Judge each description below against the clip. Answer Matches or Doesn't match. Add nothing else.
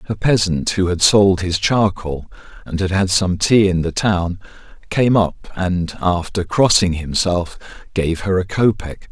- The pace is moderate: Matches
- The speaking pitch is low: Matches